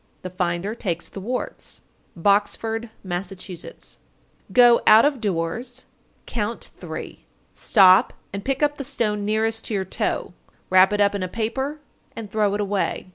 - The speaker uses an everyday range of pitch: Yes, average, 3.6 semitones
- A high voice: Yes, high, 210 Hz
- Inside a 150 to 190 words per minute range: Yes, average, 155 wpm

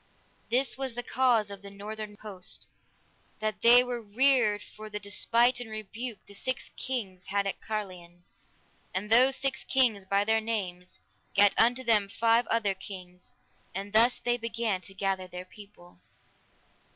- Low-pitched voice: No, high, 215 Hz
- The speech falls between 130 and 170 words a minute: Yes, average, 155 wpm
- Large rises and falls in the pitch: No, average, 3.2 semitones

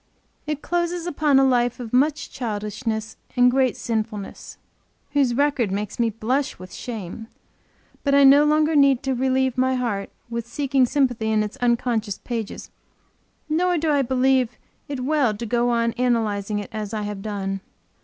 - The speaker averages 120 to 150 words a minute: No, average, 165 wpm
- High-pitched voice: Yes, high, 245 Hz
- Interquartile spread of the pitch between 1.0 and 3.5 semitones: No, average, 4.0 semitones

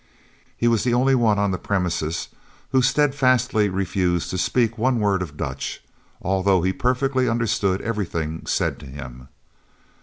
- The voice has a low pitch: Yes, low, 100 Hz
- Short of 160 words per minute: Yes, average, 150 wpm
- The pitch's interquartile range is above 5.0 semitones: Yes, wide, 5.5 semitones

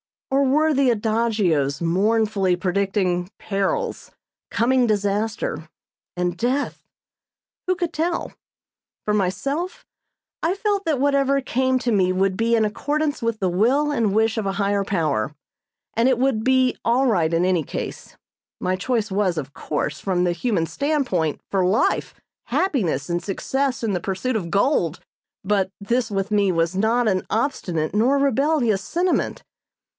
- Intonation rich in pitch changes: Yes, wide, 6.0 semitones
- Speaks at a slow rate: No, average, 150 wpm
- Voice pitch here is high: Yes, high, 215 Hz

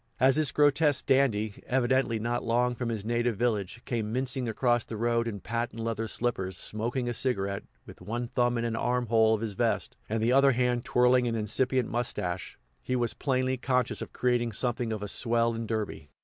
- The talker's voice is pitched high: No, low, 120 Hz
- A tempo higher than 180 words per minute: Yes, average, 195 wpm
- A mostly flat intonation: Yes, narrow, 2.0 semitones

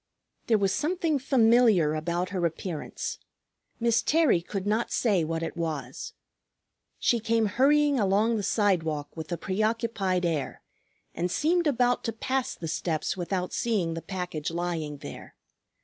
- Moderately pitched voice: No, high, 195 Hz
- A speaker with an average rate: Yes, average, 145 wpm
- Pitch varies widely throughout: Yes, wide, 5.8 semitones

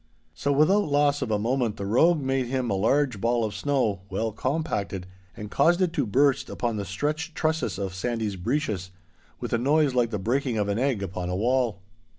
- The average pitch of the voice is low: Yes, low, 120 Hz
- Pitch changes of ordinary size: No, wide, 5.8 semitones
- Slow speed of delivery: No, average, 200 wpm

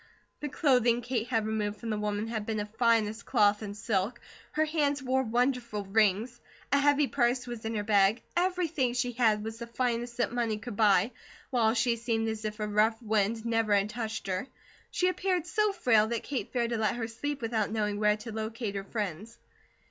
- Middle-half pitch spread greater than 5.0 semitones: No, narrow, 2.6 semitones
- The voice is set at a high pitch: Yes, high, 225 Hz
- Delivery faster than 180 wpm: Yes, average, 200 wpm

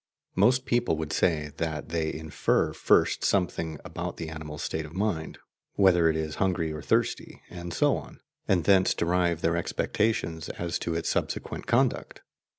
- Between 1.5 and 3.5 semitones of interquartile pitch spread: Yes, average, 2.7 semitones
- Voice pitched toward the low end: Yes, very low, 85 Hz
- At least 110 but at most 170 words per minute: Yes, average, 160 wpm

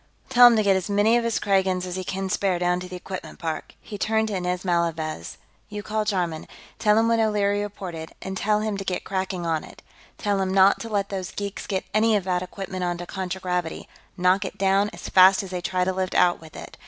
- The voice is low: No, high, 190 Hz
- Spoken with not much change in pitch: Yes, narrow, 2.3 semitones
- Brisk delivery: Yes, fast, 240 wpm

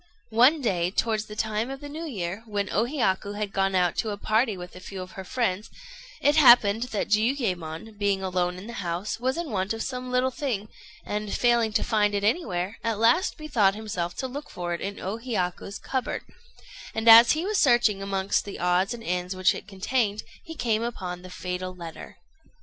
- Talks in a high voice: Yes, high, 210 Hz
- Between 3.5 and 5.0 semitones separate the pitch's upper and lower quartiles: Yes, average, 4.2 semitones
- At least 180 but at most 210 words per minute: Yes, fast, 205 wpm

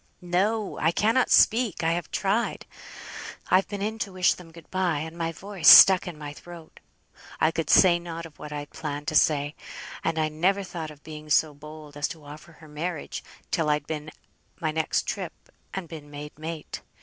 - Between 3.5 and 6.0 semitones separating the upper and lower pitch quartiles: No, average, 3.1 semitones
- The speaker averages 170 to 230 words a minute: Yes, average, 195 wpm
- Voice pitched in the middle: Yes, medium, 160 Hz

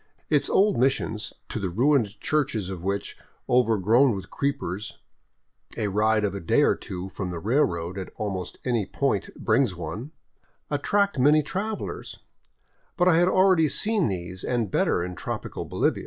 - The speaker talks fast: No, average, 155 wpm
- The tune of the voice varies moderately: No, wide, 7.1 semitones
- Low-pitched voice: Yes, low, 110 Hz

